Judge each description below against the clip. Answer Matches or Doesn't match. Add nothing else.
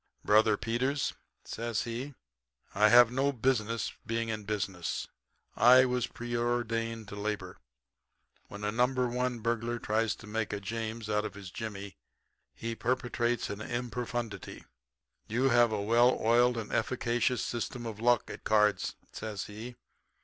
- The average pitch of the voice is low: Matches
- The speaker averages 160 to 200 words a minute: Doesn't match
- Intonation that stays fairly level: Matches